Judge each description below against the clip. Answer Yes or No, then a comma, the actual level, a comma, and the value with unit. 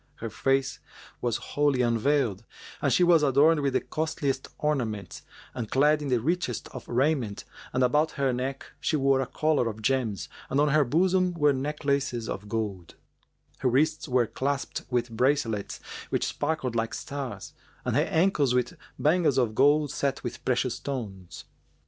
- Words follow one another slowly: No, average, 160 wpm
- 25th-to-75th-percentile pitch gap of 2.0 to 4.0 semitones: Yes, average, 3.6 semitones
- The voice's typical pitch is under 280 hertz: Yes, low, 135 Hz